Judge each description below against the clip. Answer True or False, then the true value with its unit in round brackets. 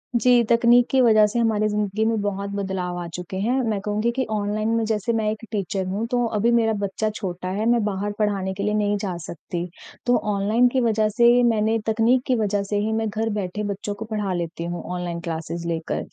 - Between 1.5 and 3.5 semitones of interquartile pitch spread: True (2.7 semitones)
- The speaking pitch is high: True (210 Hz)